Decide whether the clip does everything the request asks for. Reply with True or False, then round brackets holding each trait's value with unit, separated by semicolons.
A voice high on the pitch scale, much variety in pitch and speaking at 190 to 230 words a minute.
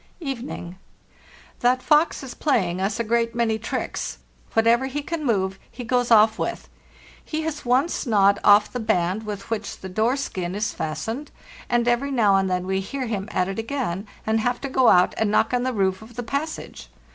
False (225 Hz; 4.5 semitones; 195 wpm)